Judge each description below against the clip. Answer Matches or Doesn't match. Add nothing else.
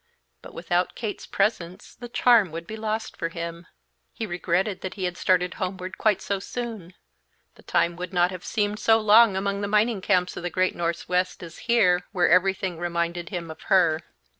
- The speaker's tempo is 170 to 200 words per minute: Matches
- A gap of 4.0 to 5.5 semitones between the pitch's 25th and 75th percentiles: Doesn't match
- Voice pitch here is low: Doesn't match